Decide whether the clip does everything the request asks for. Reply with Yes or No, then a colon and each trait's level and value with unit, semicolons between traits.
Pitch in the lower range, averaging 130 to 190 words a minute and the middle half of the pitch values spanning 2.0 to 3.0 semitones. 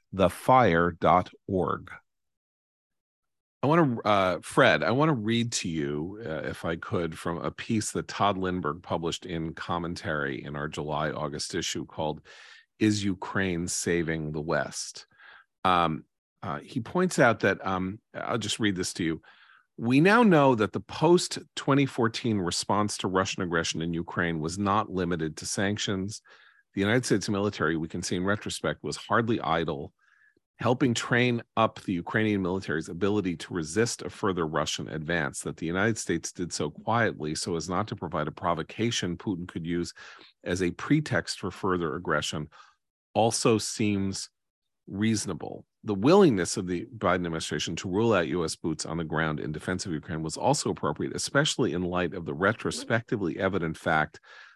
No: very low, 95 Hz; average, 160 wpm; average, 4.6 semitones